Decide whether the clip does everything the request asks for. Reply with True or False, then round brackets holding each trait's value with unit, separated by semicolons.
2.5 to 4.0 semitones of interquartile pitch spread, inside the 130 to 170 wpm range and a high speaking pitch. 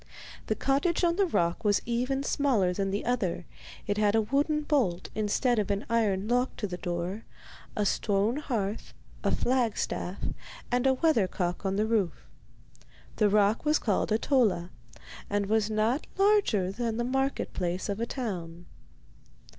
False (4.6 semitones; 160 wpm; 215 Hz)